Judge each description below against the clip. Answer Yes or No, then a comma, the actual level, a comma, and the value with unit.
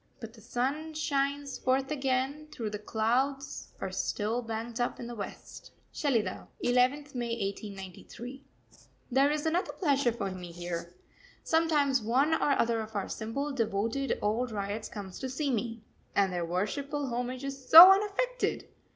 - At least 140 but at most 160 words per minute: Yes, average, 150 wpm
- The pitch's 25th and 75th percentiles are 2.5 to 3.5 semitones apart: No, average, 4.4 semitones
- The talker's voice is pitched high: Yes, high, 245 Hz